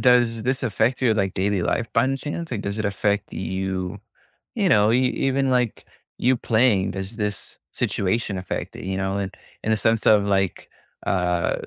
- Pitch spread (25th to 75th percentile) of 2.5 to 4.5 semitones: Yes, average, 4.2 semitones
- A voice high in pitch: No, low, 105 Hz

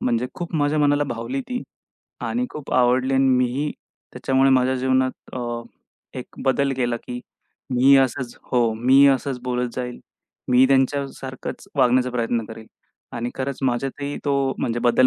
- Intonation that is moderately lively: No, narrow, 1.9 semitones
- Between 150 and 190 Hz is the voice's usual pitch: No, low, 130 Hz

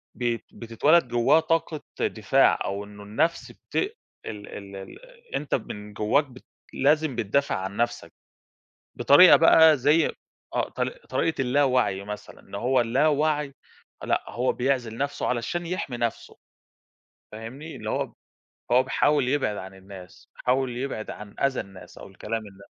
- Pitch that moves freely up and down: Yes, wide, 5.7 semitones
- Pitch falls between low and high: No, low, 125 Hz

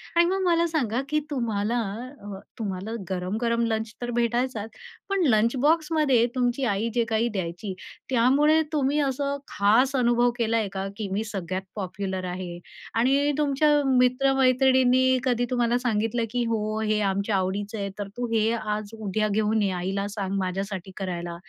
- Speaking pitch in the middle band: No, high, 225 Hz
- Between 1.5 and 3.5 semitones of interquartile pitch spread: No, average, 4.2 semitones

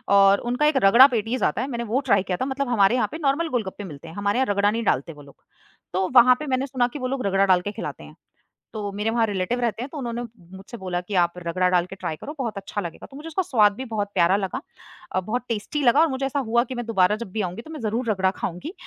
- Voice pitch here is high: Yes, high, 220 Hz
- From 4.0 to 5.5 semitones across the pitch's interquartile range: Yes, average, 4.9 semitones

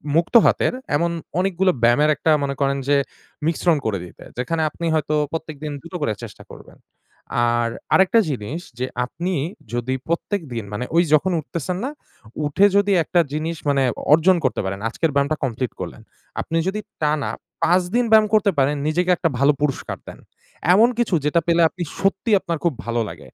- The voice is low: No, medium, 160 Hz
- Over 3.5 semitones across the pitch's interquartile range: Yes, average, 4.7 semitones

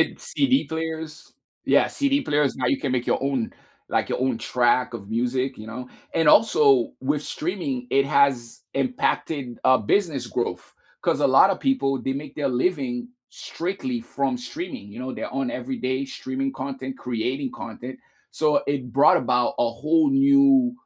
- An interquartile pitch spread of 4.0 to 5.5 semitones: Yes, average, 4.6 semitones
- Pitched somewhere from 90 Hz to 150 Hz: Yes, low, 135 Hz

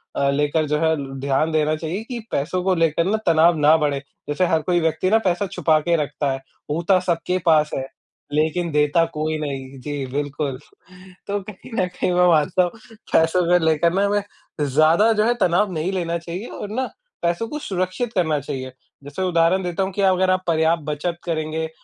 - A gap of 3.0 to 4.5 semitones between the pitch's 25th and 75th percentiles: Yes, average, 3.4 semitones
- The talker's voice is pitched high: No, medium, 165 Hz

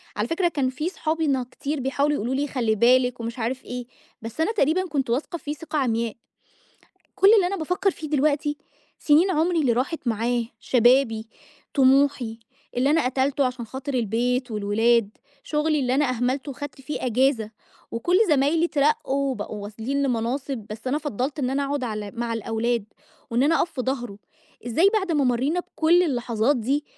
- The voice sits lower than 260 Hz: No, very high, 265 Hz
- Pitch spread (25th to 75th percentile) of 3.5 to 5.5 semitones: Yes, average, 4.0 semitones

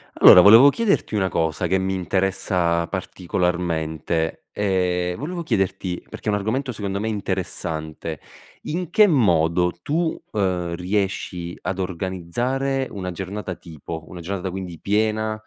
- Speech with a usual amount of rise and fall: Yes, average, 3.5 semitones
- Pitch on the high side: No, very low, 95 Hz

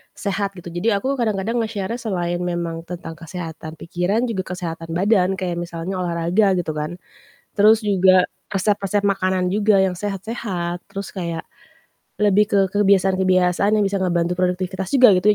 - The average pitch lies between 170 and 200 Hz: Yes, high, 190 Hz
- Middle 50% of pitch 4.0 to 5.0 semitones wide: No, narrow, 2.6 semitones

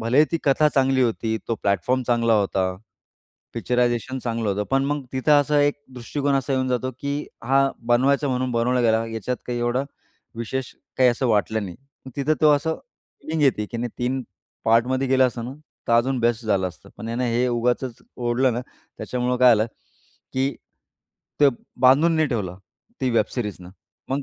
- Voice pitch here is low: Yes, low, 125 Hz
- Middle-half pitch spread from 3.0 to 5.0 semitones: No, narrow, 2.6 semitones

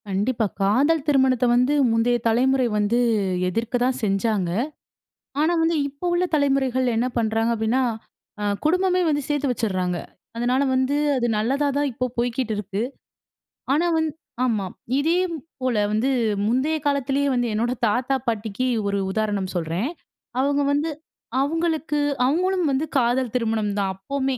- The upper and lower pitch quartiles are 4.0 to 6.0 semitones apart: Yes, average, 4.4 semitones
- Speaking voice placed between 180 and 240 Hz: No, very high, 255 Hz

